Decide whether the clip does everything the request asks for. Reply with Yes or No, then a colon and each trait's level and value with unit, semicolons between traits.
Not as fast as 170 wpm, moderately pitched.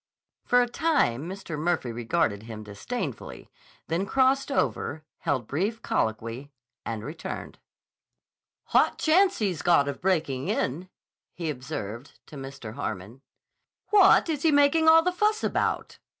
Yes: slow, 135 wpm; medium, 165 Hz